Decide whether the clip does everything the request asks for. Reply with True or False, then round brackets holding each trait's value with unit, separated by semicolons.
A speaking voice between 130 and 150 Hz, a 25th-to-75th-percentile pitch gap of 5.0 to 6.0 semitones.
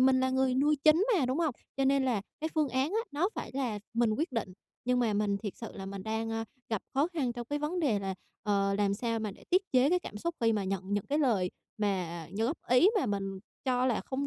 False (245 Hz; 5.3 semitones)